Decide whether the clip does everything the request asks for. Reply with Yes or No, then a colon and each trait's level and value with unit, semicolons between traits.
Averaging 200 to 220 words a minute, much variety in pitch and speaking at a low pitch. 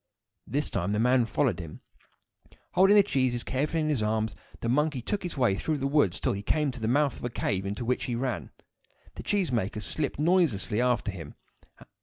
Yes: fast, 205 wpm; wide, 5.7 semitones; low, 125 Hz